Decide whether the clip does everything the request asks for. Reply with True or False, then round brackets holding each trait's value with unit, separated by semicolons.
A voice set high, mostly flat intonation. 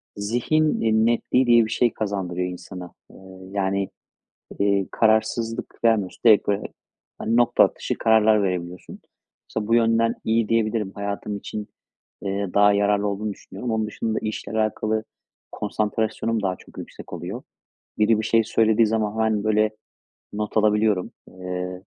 False (110 Hz; 1.8 semitones)